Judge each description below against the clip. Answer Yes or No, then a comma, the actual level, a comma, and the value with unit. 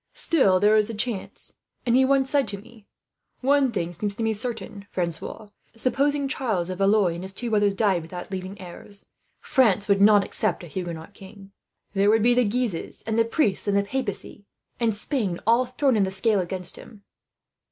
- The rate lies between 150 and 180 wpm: No, average, 200 wpm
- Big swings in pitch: No, average, 3.7 semitones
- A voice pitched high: Yes, high, 205 Hz